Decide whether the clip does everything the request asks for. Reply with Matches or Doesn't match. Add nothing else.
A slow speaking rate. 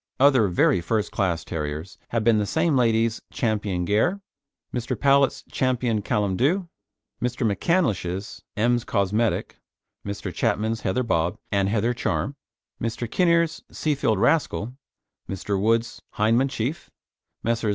Matches